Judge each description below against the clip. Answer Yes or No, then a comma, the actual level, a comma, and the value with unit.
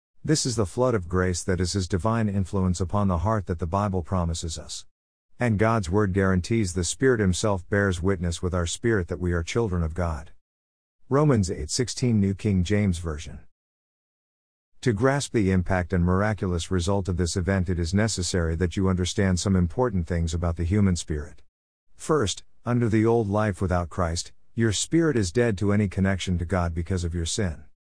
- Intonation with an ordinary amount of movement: Yes, average, 3.4 semitones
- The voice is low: Yes, very low, 95 Hz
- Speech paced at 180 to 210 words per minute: Yes, average, 185 wpm